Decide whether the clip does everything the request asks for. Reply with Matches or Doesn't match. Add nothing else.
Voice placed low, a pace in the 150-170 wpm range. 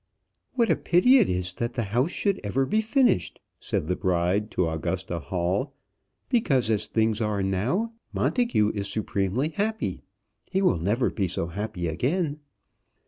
Matches